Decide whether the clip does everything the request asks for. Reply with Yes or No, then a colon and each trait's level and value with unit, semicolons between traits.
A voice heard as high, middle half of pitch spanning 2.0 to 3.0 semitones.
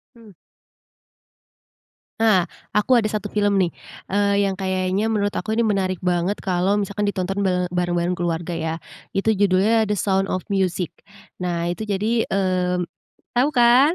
Yes: high, 195 Hz; narrow, 2.5 semitones